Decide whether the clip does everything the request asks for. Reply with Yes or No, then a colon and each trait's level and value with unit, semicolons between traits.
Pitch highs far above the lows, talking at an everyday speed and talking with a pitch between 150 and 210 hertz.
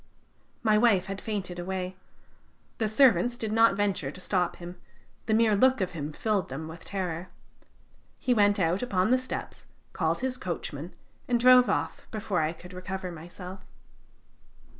No: average, 3.8 semitones; average, 160 wpm; high, 190 Hz